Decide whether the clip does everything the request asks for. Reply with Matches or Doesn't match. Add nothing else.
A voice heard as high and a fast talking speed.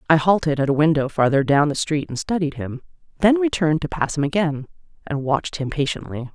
Doesn't match